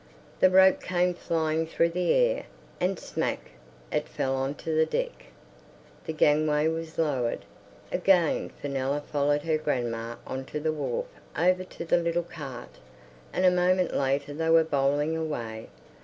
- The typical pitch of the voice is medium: Yes, medium, 160 Hz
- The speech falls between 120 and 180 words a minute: Yes, average, 155 wpm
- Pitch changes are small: No, average, 3.7 semitones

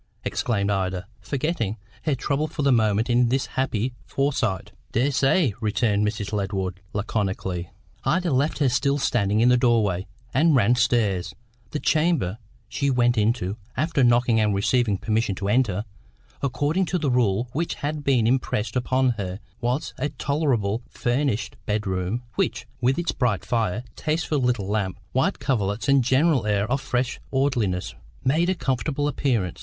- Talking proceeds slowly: No, average, 150 wpm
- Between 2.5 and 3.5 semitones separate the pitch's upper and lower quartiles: No, average, 5.0 semitones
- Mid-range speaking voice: No, low, 120 Hz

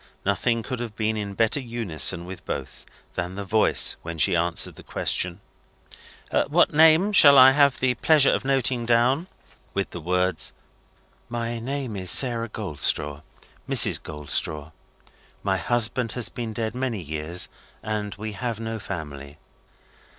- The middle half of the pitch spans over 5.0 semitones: Yes, wide, 5.5 semitones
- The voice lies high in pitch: No, low, 110 Hz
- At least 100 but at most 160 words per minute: Yes, average, 145 wpm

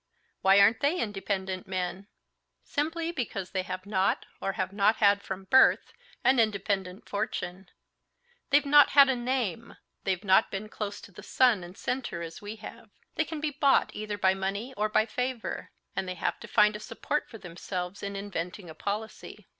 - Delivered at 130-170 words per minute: No, average, 180 wpm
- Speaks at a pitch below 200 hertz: No, high, 205 Hz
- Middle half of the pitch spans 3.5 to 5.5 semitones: Yes, average, 3.9 semitones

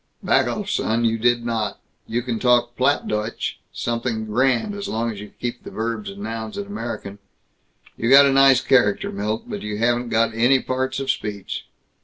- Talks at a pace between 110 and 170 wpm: No, average, 185 wpm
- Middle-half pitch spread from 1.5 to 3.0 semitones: Yes, average, 2.7 semitones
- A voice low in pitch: Yes, low, 115 Hz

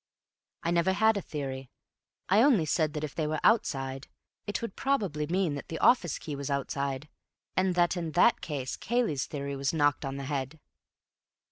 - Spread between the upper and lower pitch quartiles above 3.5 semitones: Yes, average, 5.0 semitones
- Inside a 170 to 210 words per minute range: Yes, average, 180 wpm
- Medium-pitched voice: Yes, medium, 155 Hz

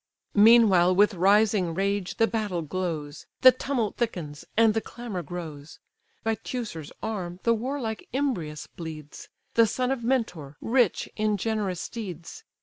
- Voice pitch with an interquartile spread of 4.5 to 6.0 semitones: Yes, average, 4.9 semitones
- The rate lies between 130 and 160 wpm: Yes, average, 140 wpm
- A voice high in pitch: Yes, high, 205 Hz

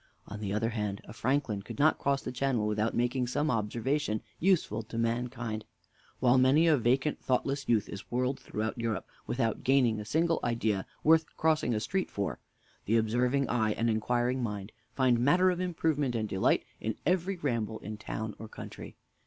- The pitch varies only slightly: No, average, 4.1 semitones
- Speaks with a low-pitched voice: Yes, low, 120 Hz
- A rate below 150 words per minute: No, average, 180 wpm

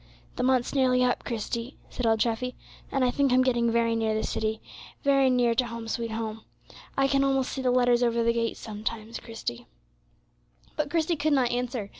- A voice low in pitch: No, high, 240 Hz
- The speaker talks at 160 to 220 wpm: Yes, average, 195 wpm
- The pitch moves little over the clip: Yes, narrow, 2.1 semitones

